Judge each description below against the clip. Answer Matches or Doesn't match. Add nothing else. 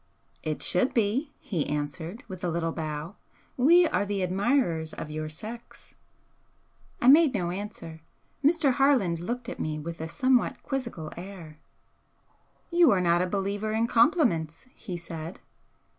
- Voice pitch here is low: Doesn't match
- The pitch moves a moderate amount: Doesn't match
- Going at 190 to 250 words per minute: Doesn't match